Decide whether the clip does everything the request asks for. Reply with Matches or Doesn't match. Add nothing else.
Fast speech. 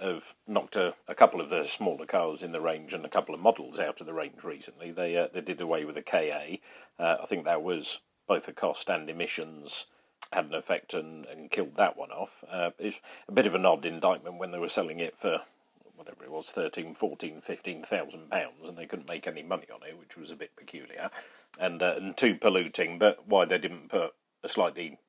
Matches